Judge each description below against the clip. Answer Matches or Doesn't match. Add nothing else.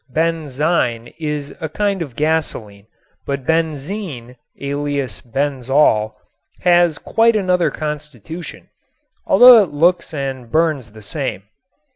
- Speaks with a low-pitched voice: Doesn't match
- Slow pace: Matches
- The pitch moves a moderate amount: Matches